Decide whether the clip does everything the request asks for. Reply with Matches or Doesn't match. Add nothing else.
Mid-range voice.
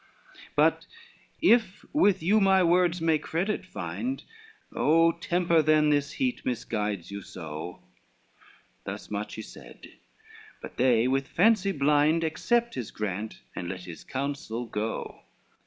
Matches